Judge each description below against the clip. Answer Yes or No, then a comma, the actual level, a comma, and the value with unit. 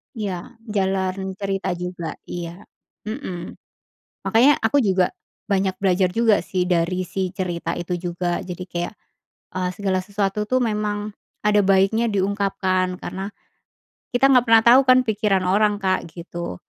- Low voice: No, high, 195 Hz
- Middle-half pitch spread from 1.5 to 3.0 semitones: Yes, narrow, 2.5 semitones